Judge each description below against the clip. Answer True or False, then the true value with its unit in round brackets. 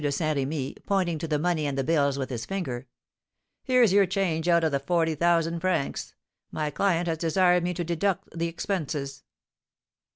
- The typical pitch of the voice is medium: True (165 Hz)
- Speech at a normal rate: True (185 wpm)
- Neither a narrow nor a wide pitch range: True (3.4 semitones)